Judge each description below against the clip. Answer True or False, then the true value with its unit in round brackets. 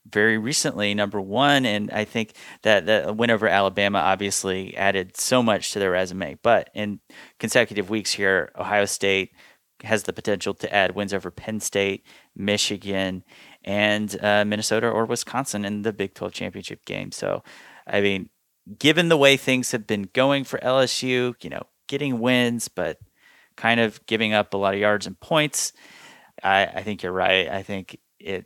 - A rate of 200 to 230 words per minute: False (175 wpm)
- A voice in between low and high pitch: False (105 Hz)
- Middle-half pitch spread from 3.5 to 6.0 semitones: False (2.7 semitones)